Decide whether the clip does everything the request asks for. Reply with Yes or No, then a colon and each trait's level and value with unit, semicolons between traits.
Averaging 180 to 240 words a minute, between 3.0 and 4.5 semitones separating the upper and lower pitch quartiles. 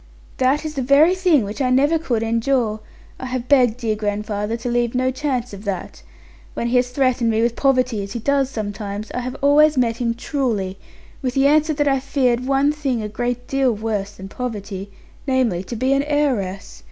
Yes: average, 200 wpm; average, 3.9 semitones